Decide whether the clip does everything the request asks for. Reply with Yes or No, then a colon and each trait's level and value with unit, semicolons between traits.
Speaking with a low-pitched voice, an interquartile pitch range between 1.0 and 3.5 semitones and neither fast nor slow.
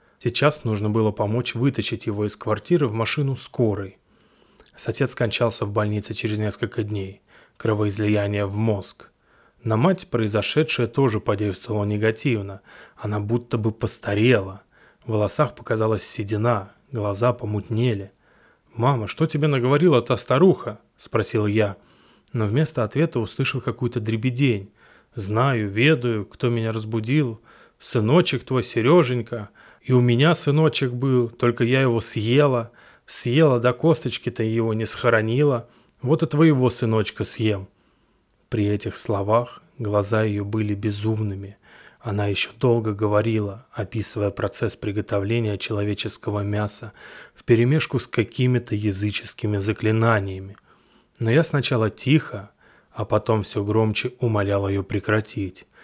Yes: low, 115 Hz; average, 2.9 semitones; average, 120 wpm